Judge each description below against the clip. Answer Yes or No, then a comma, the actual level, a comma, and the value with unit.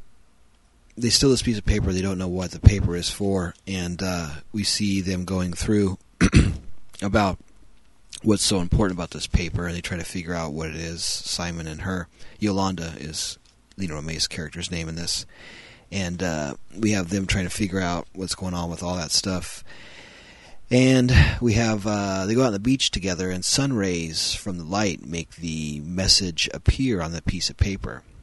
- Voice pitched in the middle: No, very low, 95 Hz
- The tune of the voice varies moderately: Yes, average, 3.0 semitones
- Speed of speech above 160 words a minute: Yes, average, 190 wpm